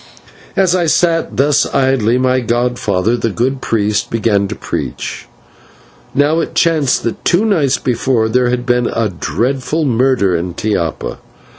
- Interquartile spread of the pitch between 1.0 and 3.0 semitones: No, average, 3.9 semitones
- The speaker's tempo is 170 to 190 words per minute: No, average, 145 wpm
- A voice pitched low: Yes, low, 125 Hz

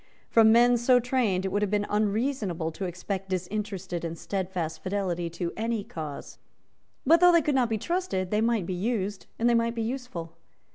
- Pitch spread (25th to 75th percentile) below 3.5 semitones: No, average, 4.4 semitones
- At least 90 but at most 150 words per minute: No, average, 190 wpm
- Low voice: No, high, 205 Hz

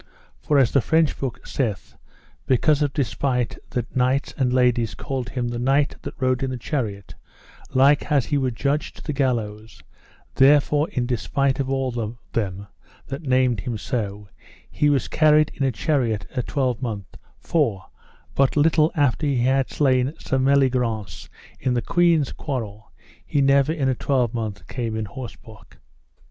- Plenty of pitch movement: No, average, 3.1 semitones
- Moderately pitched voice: No, low, 130 Hz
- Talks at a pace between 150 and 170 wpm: Yes, average, 160 wpm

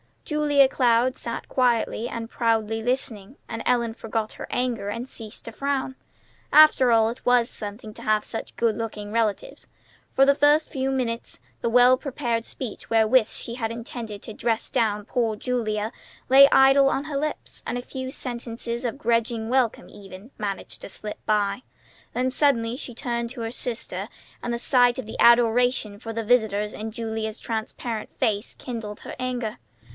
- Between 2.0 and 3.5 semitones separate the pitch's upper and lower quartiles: Yes, narrow, 2.4 semitones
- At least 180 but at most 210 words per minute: No, average, 170 wpm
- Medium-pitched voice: No, high, 235 Hz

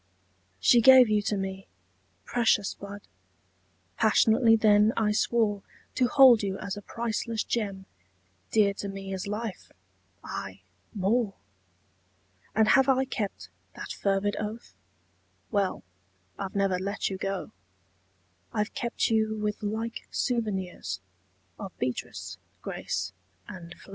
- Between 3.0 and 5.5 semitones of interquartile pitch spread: No, narrow, 2.5 semitones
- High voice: Yes, high, 210 Hz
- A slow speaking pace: Yes, slow, 125 wpm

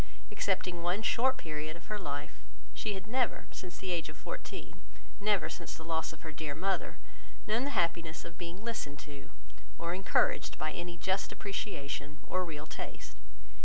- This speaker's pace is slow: No, average, 170 wpm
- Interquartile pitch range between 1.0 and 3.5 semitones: No, average, 4.0 semitones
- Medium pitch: Yes, medium, 170 Hz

